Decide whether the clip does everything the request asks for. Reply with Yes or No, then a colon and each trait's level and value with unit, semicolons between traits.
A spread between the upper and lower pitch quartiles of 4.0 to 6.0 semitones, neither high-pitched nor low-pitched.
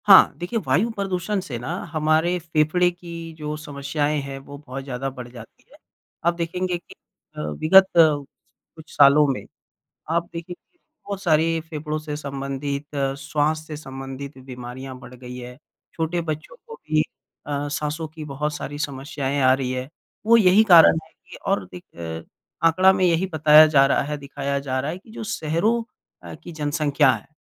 No: average, 3.5 semitones; medium, 150 Hz